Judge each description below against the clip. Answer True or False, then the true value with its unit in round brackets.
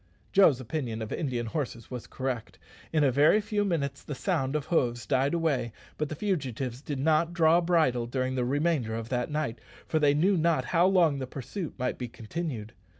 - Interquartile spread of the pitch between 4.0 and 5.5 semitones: True (4.8 semitones)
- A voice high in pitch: False (140 Hz)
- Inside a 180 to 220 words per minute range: True (195 wpm)